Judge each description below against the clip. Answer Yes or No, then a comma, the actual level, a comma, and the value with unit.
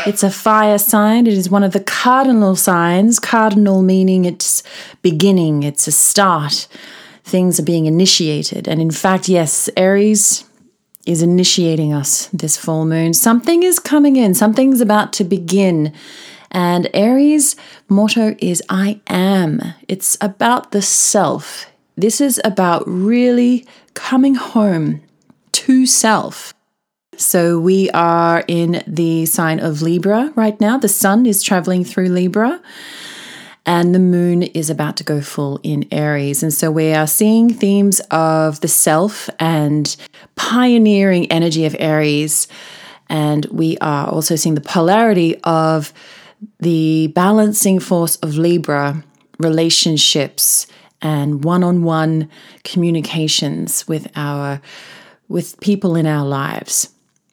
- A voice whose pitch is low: No, medium, 180 Hz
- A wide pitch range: No, average, 4.7 semitones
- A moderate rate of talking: No, slow, 130 wpm